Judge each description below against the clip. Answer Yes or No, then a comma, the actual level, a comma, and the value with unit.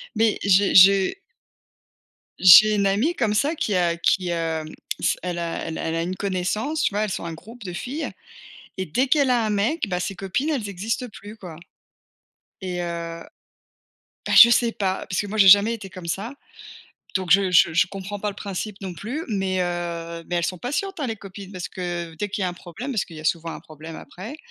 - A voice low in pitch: No, high, 195 Hz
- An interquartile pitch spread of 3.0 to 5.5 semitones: Yes, average, 3.7 semitones